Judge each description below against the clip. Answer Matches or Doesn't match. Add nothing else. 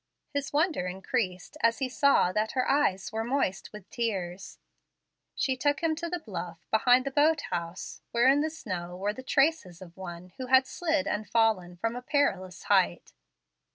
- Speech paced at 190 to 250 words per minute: Doesn't match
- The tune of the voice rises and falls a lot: Matches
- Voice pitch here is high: Matches